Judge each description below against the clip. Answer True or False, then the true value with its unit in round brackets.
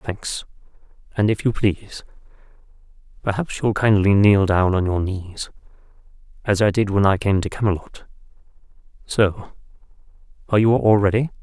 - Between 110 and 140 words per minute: True (135 wpm)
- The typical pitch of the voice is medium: False (100 Hz)